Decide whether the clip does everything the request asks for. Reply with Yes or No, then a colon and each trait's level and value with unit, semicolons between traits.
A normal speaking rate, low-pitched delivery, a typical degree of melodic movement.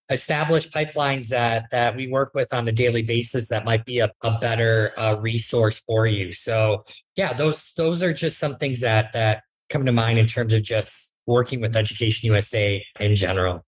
Yes: average, 195 wpm; low, 115 Hz; average, 3.0 semitones